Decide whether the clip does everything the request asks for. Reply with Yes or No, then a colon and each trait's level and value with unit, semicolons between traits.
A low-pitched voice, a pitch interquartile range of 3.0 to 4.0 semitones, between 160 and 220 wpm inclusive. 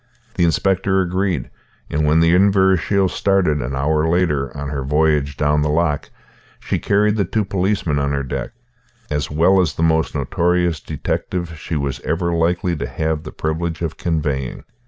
Yes: very low, 80 Hz; average, 3.5 semitones; average, 170 wpm